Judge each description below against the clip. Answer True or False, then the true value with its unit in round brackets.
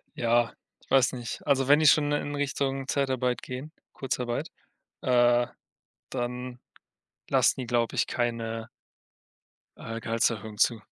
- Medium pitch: False (125 Hz)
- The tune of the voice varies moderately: False (2.3 semitones)